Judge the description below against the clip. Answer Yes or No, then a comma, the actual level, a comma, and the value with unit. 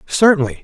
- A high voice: No, medium, 175 Hz